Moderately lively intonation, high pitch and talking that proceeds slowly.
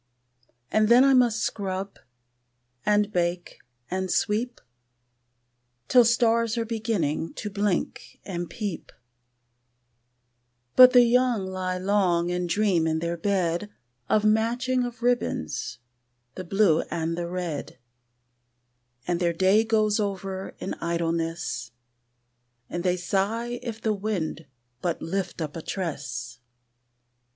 Yes: average, 4.5 semitones; high, 195 Hz; slow, 120 wpm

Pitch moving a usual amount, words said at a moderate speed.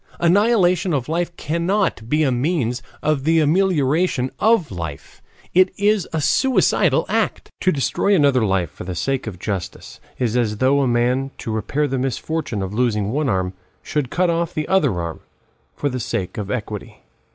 No: wide, 7.3 semitones; average, 175 wpm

